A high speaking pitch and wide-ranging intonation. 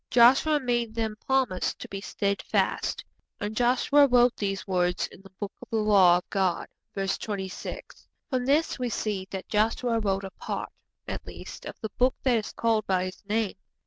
No: high, 215 Hz; average, 4.0 semitones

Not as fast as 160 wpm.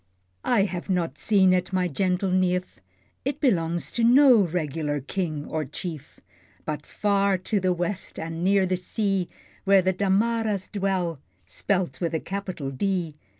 Yes: average, 150 wpm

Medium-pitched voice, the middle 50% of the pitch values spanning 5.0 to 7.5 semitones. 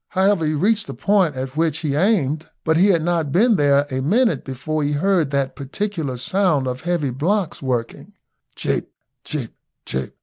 Yes: medium, 155 Hz; wide, 5.4 semitones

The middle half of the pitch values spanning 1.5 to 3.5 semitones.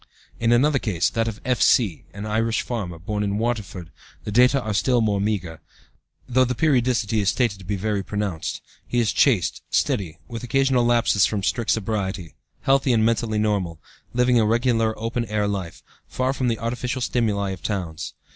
Yes: average, 3.2 semitones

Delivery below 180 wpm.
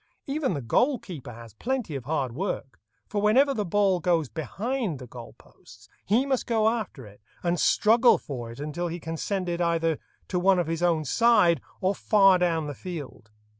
No: average, 195 wpm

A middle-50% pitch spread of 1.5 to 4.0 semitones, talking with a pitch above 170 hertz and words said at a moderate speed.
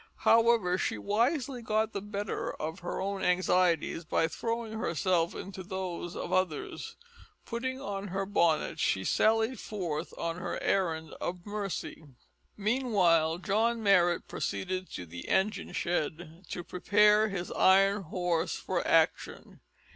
No: average, 3.6 semitones; high, 190 Hz; slow, 130 wpm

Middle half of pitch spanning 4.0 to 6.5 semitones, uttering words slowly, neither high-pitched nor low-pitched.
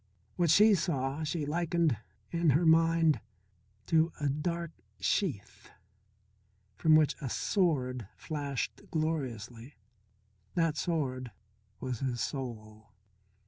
Yes: average, 4.4 semitones; slow, 100 wpm; medium, 150 Hz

